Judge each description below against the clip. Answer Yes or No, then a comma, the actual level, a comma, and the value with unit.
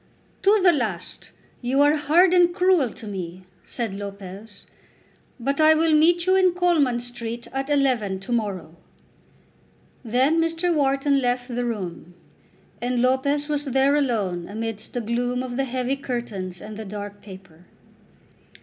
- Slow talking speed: No, average, 150 wpm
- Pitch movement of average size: No, wide, 5.8 semitones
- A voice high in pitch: Yes, high, 245 Hz